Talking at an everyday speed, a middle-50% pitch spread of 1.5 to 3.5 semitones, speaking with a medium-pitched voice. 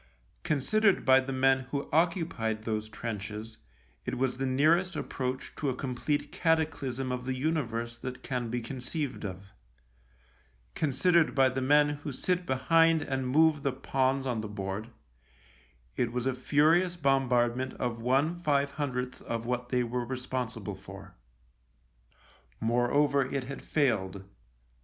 No: average, 145 wpm; average, 3.2 semitones; low, 130 Hz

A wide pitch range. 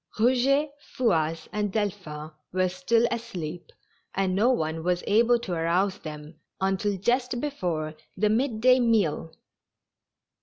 Yes: wide, 5.9 semitones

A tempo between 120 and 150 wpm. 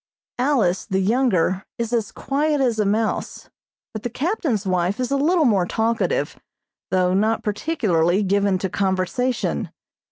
Yes: average, 140 wpm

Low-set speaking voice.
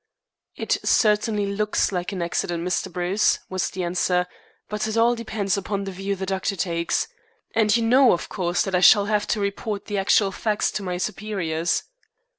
No: high, 200 Hz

